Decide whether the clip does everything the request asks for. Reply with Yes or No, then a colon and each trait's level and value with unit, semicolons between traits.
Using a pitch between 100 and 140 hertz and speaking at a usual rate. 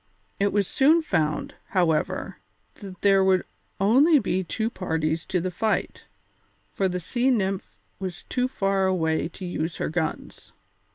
No: high, 190 Hz; average, 150 wpm